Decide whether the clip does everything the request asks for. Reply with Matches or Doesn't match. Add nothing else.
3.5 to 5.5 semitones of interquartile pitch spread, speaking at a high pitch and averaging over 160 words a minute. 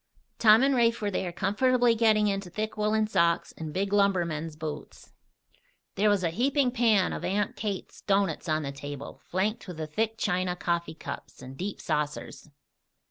Matches